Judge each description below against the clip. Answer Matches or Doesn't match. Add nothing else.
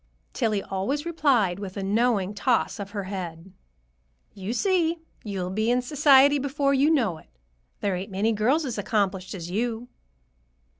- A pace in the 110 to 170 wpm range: Matches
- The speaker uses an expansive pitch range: Matches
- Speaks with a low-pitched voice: Doesn't match